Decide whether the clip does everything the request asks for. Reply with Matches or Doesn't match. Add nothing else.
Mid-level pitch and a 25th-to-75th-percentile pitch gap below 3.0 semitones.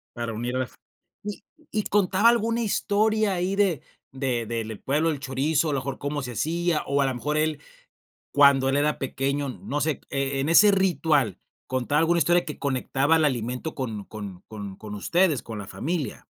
Doesn't match